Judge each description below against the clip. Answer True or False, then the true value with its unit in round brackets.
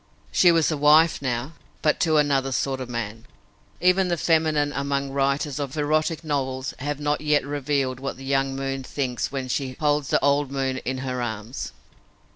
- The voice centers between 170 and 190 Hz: False (140 Hz)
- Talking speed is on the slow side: False (180 wpm)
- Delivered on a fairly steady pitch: True (2.1 semitones)